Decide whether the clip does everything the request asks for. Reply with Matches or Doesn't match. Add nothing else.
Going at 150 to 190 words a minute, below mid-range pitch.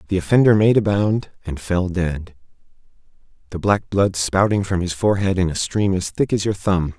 Doesn't match